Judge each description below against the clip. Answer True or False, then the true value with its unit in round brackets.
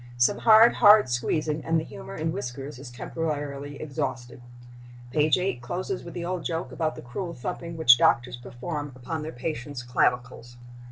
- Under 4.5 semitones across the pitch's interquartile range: False (5.1 semitones)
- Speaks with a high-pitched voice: False (145 Hz)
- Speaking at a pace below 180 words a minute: True (165 wpm)